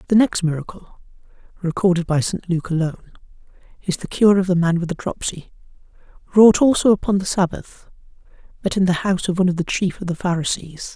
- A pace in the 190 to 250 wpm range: No, average, 175 wpm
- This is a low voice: No, medium, 180 Hz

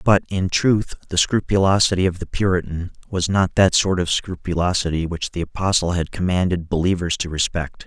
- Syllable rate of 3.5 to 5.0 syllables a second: No, 5.3 syllables/s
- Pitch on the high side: No, very low, 90 Hz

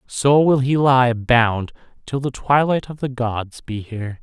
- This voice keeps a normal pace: Yes, average, 185 wpm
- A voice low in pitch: Yes, low, 125 Hz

